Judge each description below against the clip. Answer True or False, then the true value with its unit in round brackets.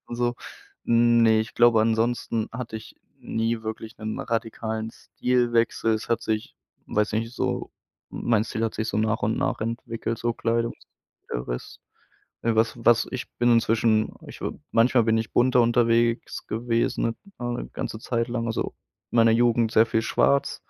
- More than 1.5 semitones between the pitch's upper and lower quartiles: False (1.1 semitones)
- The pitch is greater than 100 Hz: True (115 Hz)